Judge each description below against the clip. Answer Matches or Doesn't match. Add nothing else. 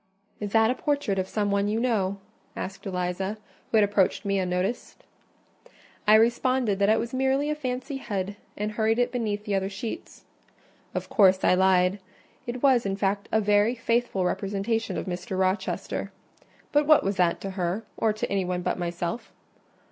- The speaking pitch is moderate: Doesn't match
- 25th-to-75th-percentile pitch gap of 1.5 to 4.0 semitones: Matches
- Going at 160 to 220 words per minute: Matches